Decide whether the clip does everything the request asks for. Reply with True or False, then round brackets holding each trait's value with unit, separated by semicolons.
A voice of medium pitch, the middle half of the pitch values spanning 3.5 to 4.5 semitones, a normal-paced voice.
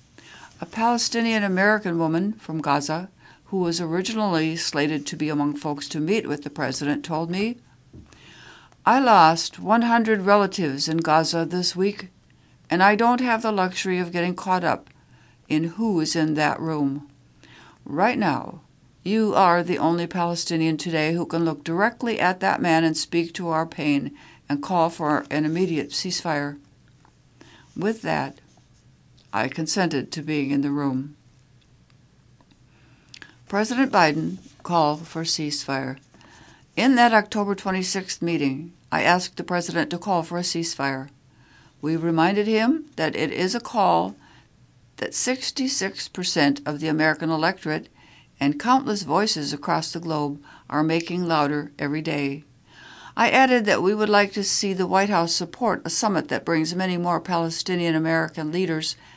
True (165 Hz; 3.9 semitones; 150 wpm)